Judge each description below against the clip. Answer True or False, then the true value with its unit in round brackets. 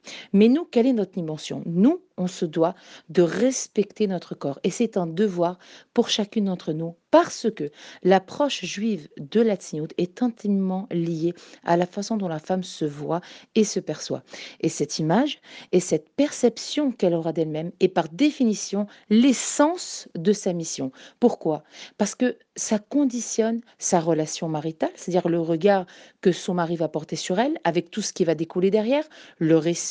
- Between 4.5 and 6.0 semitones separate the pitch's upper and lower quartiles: True (5.4 semitones)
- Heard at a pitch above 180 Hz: True (190 Hz)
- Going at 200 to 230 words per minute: False (175 wpm)